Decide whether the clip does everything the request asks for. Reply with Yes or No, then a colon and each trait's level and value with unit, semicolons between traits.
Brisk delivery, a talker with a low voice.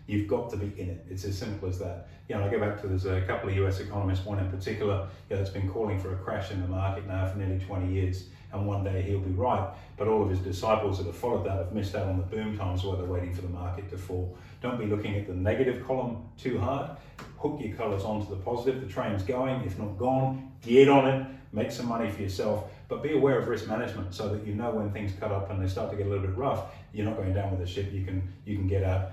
Yes: fast, 280 wpm; low, 100 Hz